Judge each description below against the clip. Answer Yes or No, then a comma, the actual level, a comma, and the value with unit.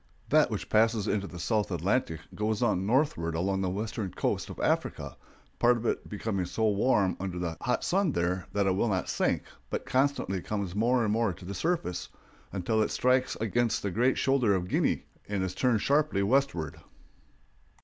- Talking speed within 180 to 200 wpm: Yes, average, 185 wpm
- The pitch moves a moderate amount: Yes, average, 4.4 semitones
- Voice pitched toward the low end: Yes, low, 105 Hz